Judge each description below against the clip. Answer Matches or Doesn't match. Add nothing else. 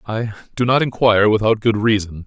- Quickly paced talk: Doesn't match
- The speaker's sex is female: Doesn't match